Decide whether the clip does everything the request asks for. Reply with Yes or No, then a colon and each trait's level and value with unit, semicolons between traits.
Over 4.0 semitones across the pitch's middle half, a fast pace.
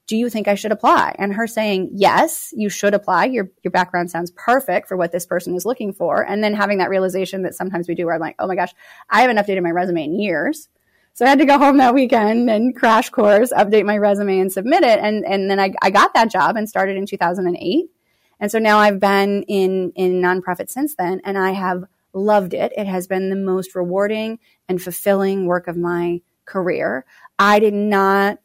No: average, 2.9 semitones; fast, 225 wpm